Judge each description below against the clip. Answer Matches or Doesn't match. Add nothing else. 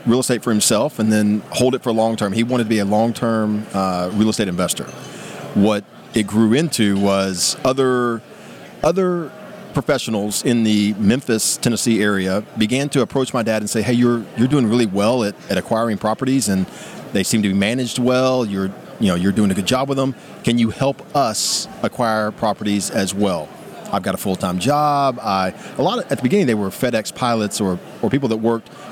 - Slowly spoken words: Doesn't match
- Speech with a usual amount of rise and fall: Matches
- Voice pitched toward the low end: Matches